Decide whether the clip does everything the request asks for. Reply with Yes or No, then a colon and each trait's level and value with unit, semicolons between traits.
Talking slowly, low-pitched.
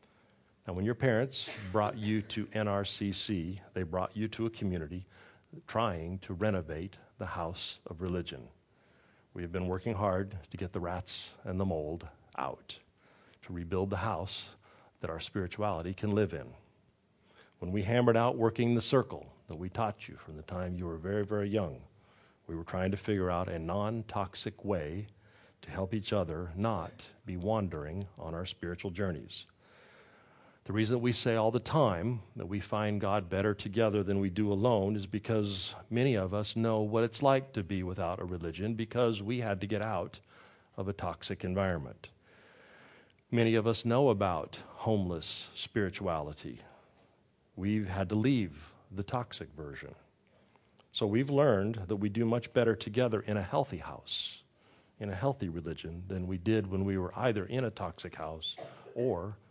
No: average, 170 wpm; low, 100 Hz